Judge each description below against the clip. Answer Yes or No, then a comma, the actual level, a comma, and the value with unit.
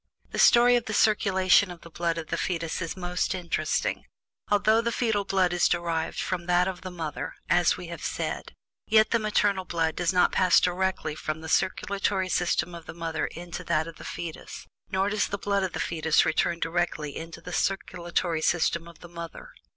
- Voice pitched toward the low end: No, medium, 175 Hz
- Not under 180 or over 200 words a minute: Yes, average, 195 wpm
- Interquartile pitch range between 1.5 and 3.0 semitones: Yes, narrow, 2.5 semitones